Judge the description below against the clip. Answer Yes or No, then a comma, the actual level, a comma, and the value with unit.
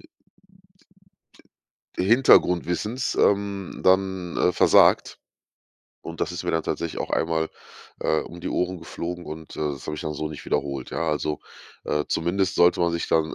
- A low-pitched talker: Yes, very low, 85 Hz